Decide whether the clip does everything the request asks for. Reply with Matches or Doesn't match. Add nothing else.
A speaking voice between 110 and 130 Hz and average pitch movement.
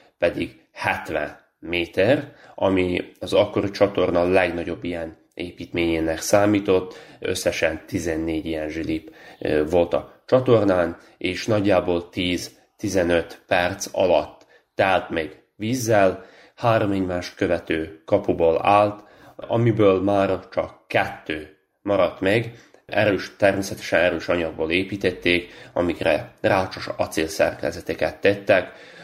Doesn't match